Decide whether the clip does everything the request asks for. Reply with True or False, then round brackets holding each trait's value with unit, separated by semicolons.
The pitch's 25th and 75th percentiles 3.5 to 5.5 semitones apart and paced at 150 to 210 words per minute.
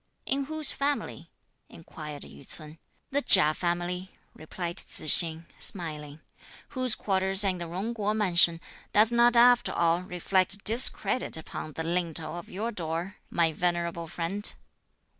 False (4.2 semitones; 140 wpm)